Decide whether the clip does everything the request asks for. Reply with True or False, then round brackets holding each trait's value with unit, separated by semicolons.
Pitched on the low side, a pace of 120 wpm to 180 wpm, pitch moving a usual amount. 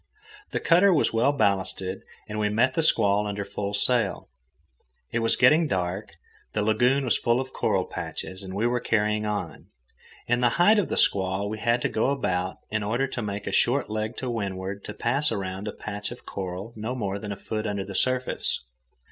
False (105 Hz; 200 wpm; 3.6 semitones)